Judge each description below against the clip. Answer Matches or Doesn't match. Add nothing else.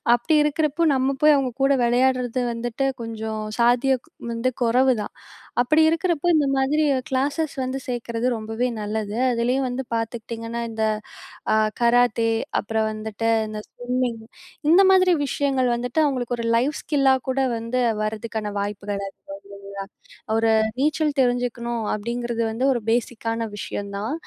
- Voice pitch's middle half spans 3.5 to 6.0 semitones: Doesn't match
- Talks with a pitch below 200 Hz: Doesn't match